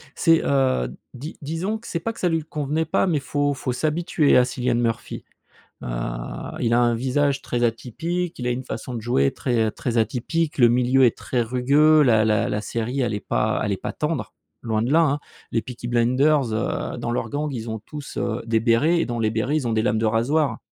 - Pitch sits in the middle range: No, low, 125 Hz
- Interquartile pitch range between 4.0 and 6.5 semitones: Yes, average, 4.5 semitones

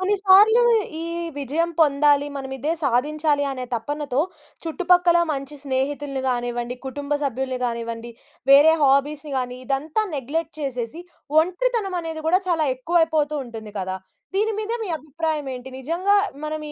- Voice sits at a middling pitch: No, very high, 290 Hz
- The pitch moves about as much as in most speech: Yes, average, 4.0 semitones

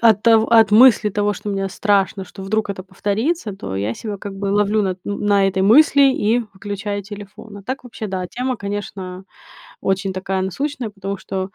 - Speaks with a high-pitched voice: Yes, high, 205 Hz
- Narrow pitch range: Yes, narrow, 2.2 semitones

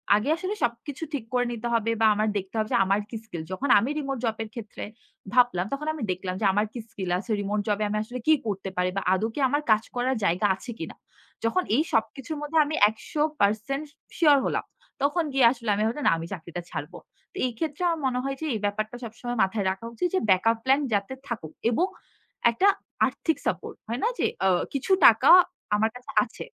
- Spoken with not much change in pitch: No, average, 4.9 semitones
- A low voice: No, high, 230 Hz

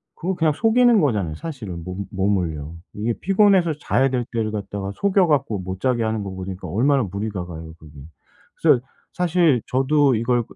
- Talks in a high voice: No, low, 115 Hz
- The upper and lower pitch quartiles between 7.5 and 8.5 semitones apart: Yes, wide, 8.0 semitones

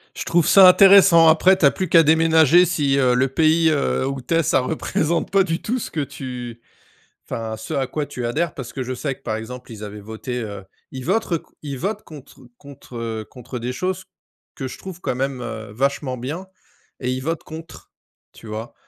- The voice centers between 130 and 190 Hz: Yes, medium, 140 Hz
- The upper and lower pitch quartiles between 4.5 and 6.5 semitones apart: Yes, average, 5.0 semitones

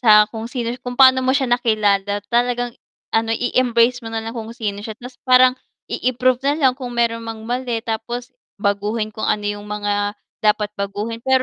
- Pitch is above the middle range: Yes, high, 230 Hz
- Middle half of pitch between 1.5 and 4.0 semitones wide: Yes, average, 2.7 semitones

